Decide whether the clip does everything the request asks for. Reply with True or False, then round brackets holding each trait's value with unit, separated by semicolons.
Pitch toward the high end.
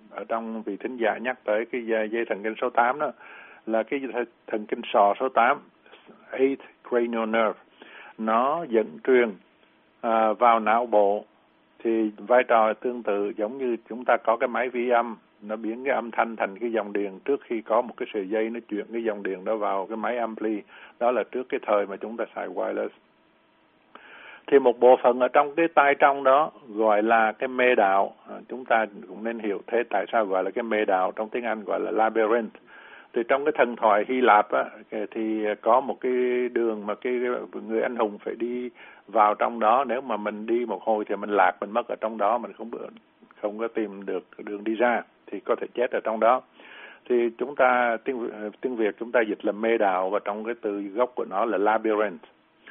False (115 Hz)